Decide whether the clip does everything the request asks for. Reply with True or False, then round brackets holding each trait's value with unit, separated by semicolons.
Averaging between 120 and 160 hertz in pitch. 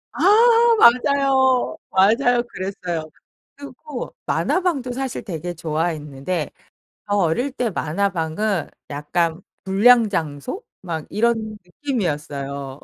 False (195 Hz)